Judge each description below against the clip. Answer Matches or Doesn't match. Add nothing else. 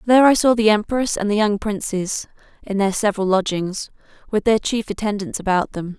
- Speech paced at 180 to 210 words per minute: Matches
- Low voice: Doesn't match